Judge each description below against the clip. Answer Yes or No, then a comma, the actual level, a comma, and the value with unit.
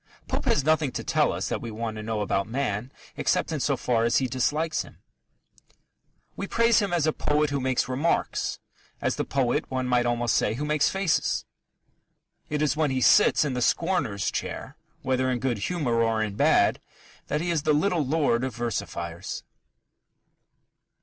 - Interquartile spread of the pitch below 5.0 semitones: Yes, average, 4.5 semitones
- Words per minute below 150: No, average, 185 wpm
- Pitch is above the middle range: No, low, 130 Hz